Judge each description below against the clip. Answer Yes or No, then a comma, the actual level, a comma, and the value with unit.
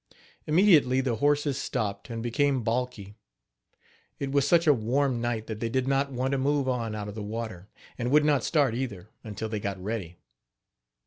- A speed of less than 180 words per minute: No, average, 185 wpm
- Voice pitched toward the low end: Yes, low, 125 Hz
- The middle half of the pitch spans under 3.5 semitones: No, average, 4.1 semitones